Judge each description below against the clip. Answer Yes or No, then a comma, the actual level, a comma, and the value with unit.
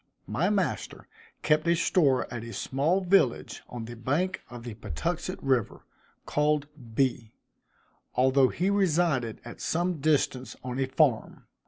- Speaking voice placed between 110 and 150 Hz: Yes, low, 135 Hz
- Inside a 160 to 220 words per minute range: No, average, 140 wpm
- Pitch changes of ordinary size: No, wide, 5.7 semitones